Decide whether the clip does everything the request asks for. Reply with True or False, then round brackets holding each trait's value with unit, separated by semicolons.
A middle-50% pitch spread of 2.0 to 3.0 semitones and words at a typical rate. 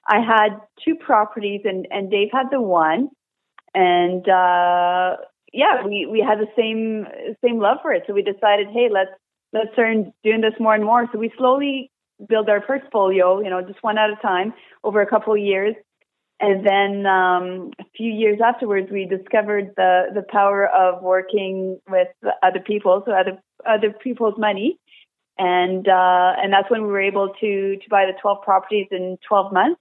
True (2.6 semitones; 185 wpm)